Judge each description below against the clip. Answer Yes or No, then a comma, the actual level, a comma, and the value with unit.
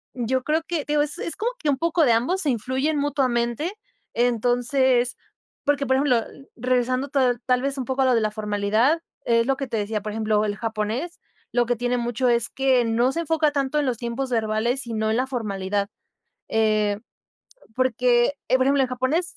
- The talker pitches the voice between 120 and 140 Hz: No, very high, 250 Hz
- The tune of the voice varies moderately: Yes, average, 3.3 semitones